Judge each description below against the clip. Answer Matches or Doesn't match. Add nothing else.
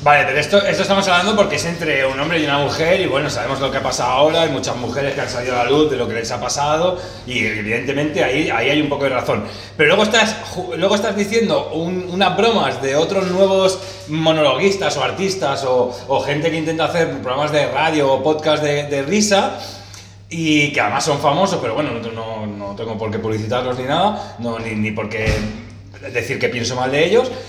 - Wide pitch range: Matches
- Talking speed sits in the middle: Doesn't match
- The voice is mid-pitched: Matches